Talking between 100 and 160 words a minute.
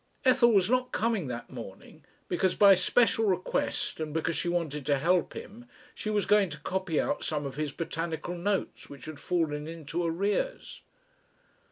No: average, 170 wpm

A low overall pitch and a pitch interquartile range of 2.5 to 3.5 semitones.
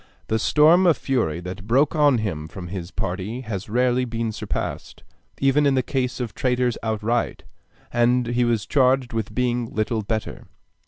Yes: low, 120 Hz; average, 3.0 semitones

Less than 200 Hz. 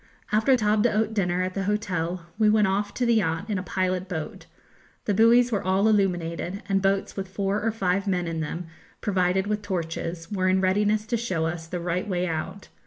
Yes: high, 190 Hz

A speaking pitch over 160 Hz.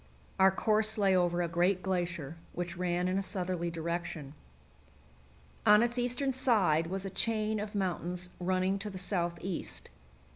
Yes: medium, 185 Hz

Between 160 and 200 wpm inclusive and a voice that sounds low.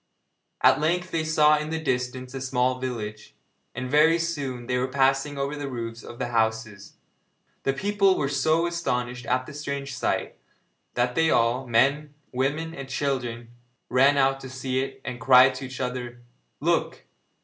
Yes: average, 170 wpm; low, 130 Hz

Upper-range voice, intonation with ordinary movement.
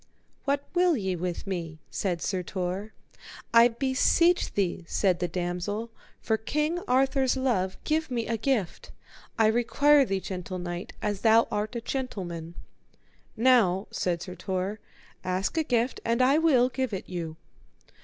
No: high, 220 Hz; wide, 6.1 semitones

